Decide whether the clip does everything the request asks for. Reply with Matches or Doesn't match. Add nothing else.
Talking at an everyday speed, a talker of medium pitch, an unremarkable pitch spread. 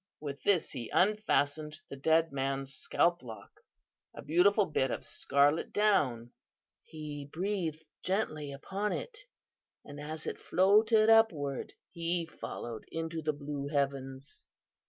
Doesn't match